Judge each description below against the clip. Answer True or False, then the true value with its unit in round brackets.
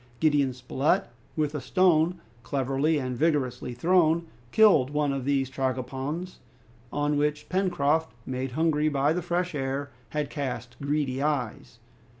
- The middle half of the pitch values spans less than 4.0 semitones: True (3.1 semitones)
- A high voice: False (145 Hz)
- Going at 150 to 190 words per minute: False (135 wpm)